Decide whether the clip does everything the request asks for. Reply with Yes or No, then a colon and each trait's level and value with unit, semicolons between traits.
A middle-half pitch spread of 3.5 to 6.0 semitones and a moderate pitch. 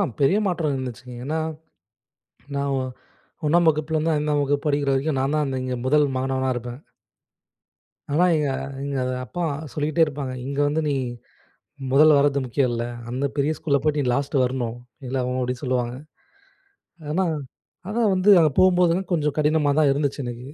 No: average, 2.9 semitones; medium, 145 Hz